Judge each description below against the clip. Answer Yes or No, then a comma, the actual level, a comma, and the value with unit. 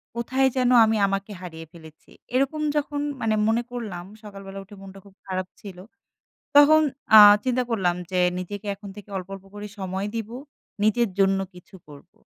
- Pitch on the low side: No, high, 200 Hz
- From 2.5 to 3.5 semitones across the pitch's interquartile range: No, average, 3.9 semitones